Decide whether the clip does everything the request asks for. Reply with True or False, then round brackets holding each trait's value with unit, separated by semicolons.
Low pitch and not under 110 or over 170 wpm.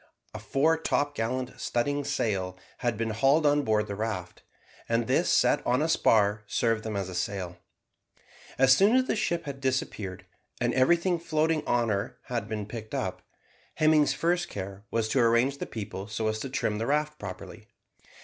False (120 Hz; 180 wpm)